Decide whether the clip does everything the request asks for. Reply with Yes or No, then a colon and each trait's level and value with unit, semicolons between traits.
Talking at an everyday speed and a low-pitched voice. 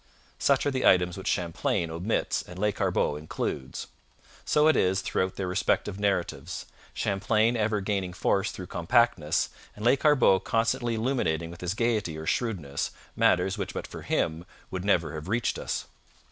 Yes: average, 155 wpm; very low, 95 Hz